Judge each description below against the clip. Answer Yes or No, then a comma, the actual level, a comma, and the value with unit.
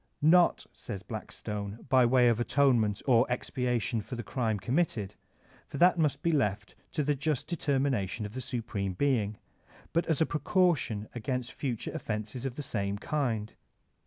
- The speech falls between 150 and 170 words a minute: Yes, average, 160 wpm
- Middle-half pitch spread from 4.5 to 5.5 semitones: Yes, average, 4.8 semitones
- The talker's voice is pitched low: Yes, low, 125 Hz